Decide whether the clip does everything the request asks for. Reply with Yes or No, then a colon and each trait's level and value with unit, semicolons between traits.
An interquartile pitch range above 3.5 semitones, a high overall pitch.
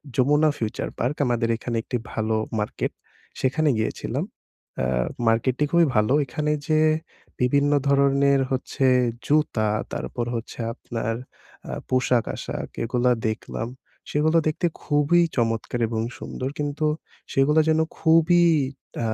No: average, 4.4 semitones; low, 135 Hz